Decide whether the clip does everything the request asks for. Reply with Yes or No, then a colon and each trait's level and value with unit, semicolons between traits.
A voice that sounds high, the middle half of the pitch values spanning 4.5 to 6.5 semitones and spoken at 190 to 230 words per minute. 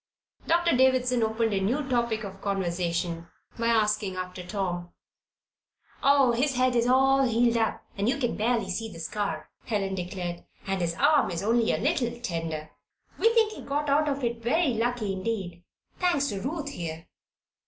No: high, 230 Hz; wide, 5.5 semitones; average, 170 wpm